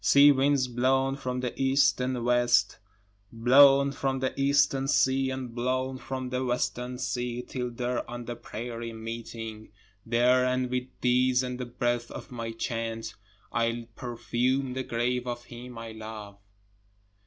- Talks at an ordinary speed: Yes, average, 150 wpm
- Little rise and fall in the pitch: Yes, narrow, 1.8 semitones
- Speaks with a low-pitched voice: Yes, low, 125 Hz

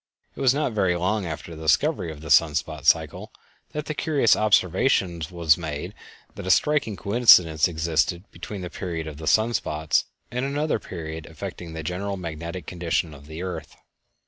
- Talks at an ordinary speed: Yes, average, 175 wpm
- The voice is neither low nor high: No, very low, 85 Hz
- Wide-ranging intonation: No, average, 4.9 semitones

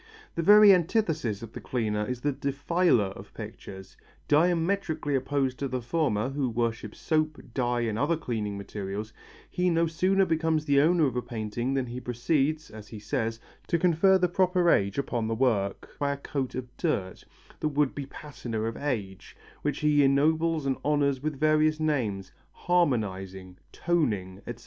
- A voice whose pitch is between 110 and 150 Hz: Yes, medium, 140 Hz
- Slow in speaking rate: No, average, 170 wpm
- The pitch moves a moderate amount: No, wide, 5.8 semitones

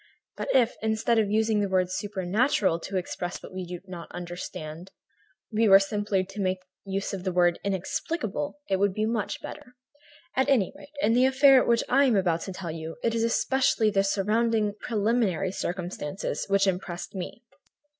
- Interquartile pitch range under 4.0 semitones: Yes, average, 3.6 semitones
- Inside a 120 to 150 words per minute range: No, average, 180 wpm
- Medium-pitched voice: No, high, 200 Hz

